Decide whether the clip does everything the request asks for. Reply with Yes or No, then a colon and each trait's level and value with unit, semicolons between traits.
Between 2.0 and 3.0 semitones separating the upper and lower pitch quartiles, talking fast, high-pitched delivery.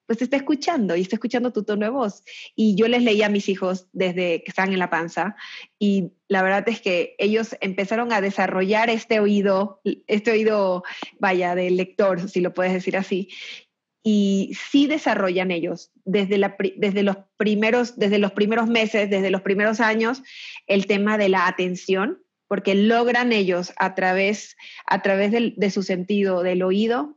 No: narrow, 2.6 semitones; average, 175 wpm; high, 200 Hz